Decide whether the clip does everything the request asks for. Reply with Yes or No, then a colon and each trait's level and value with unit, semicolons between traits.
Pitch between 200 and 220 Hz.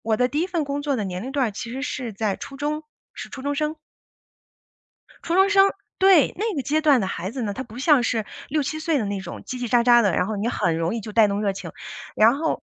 No: very high, 250 Hz